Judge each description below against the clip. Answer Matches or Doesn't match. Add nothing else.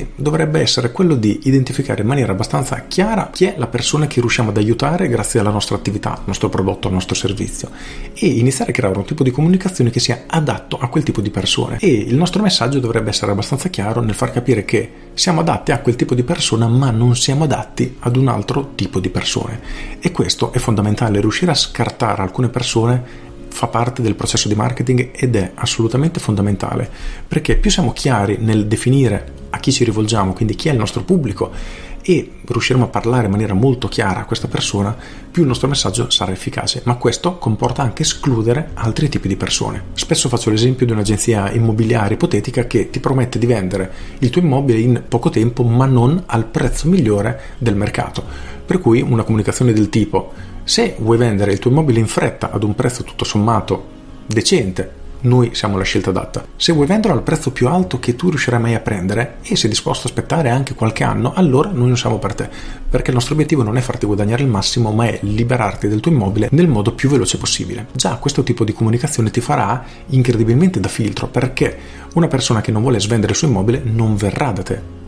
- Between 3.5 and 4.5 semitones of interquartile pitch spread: Matches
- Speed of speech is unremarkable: Doesn't match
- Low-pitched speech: Matches